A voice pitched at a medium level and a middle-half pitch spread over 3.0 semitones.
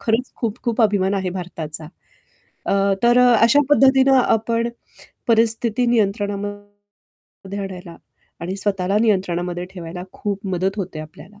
No: high, 205 Hz; average, 3.8 semitones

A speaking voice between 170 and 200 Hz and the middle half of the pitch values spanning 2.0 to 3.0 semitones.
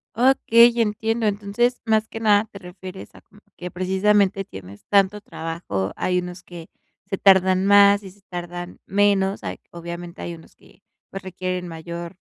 Yes: high, 190 Hz; average, 2.7 semitones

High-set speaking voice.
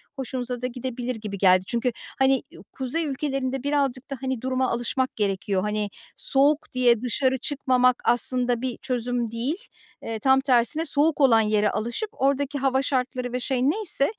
Yes: very high, 255 Hz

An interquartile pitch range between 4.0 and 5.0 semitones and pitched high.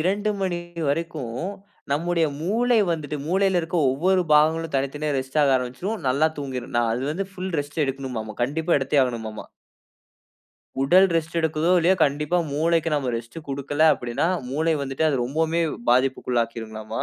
No: average, 4.3 semitones; medium, 150 Hz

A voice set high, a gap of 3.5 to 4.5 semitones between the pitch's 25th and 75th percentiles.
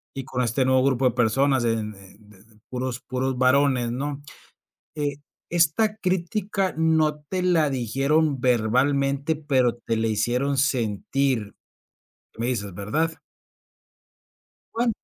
No: low, 130 Hz; average, 4.1 semitones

